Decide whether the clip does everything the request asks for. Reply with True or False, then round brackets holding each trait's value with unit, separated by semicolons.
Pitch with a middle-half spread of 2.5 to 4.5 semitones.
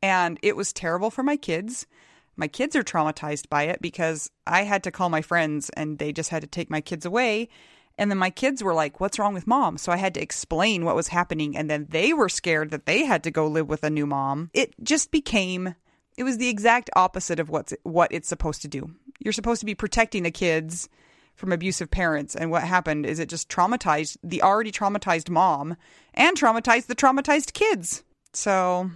False (5.2 semitones)